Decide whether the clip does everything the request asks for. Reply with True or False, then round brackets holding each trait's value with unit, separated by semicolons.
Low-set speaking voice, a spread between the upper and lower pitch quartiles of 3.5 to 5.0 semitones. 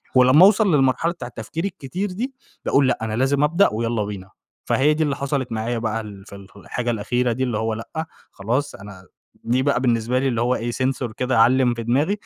True (125 Hz; 4.0 semitones)